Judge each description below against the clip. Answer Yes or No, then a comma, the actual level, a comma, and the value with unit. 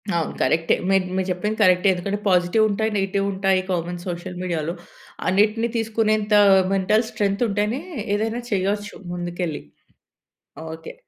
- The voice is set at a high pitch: Yes, high, 195 Hz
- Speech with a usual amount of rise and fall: Yes, average, 3.1 semitones